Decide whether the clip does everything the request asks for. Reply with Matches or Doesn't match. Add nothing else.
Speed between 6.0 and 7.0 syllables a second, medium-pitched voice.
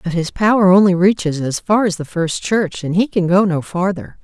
Doesn't match